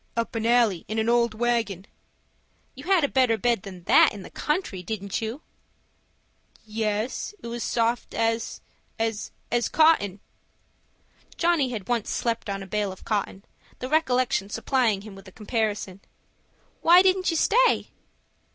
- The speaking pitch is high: Yes, high, 225 Hz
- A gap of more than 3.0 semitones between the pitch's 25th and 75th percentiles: Yes, average, 3.5 semitones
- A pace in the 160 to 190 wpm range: No, average, 150 wpm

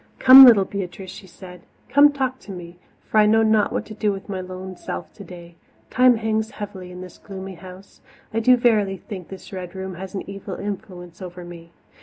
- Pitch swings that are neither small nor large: Yes, average, 3.0 semitones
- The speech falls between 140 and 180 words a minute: No, fast, 205 wpm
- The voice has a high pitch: Yes, high, 195 Hz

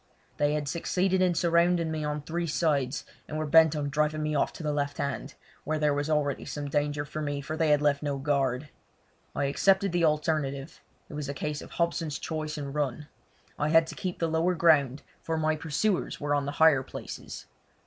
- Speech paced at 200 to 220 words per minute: Yes, fast, 205 wpm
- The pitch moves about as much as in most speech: No, narrow, 2.1 semitones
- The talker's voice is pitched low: No, medium, 150 Hz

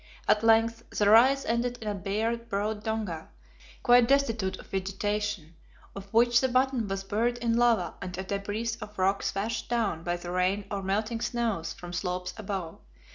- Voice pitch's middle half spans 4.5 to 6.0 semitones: No, average, 3.3 semitones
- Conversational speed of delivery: Yes, average, 175 wpm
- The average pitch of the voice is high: Yes, high, 210 Hz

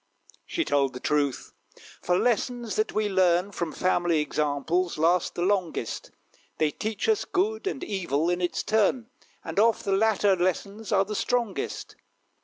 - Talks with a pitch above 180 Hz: Yes, high, 190 Hz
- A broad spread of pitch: No, average, 4.3 semitones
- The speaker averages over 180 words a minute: No, average, 155 wpm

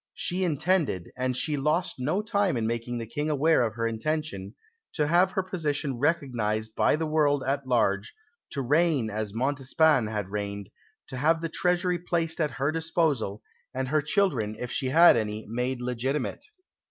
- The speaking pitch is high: No, medium, 140 Hz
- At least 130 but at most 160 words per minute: No, average, 170 wpm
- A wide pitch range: Yes, wide, 5.7 semitones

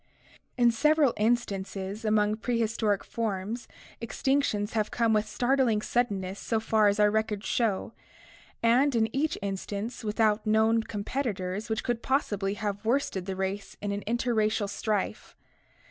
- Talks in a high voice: Yes, high, 220 Hz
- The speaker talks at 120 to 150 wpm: Yes, slow, 135 wpm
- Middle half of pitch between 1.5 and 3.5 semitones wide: Yes, narrow, 2.4 semitones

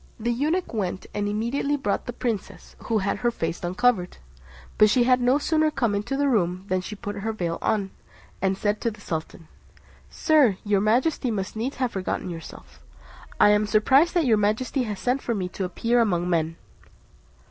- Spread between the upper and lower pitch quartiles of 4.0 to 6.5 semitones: Yes, average, 4.7 semitones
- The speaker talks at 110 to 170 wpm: No, average, 190 wpm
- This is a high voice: Yes, high, 215 Hz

